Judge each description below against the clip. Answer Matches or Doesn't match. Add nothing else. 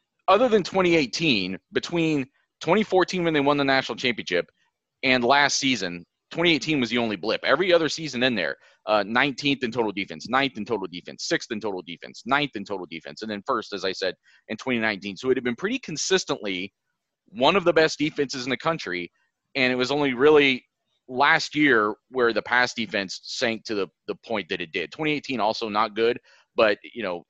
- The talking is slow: Doesn't match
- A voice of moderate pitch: Doesn't match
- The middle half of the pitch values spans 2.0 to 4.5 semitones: Doesn't match